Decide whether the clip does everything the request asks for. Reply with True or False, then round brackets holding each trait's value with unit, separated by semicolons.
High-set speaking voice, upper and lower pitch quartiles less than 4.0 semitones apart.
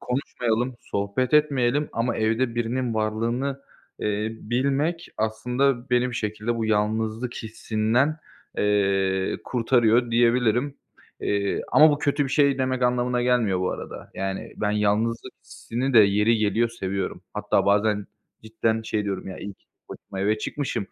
False (115 Hz; 3.0 semitones)